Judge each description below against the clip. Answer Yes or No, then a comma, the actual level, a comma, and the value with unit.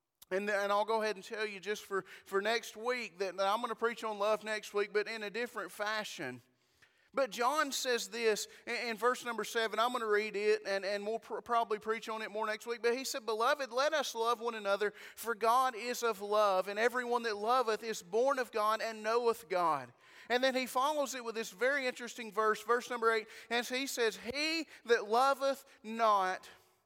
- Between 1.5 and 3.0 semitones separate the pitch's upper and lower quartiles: Yes, narrow, 2.4 semitones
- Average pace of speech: No, fast, 220 wpm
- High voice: Yes, high, 225 Hz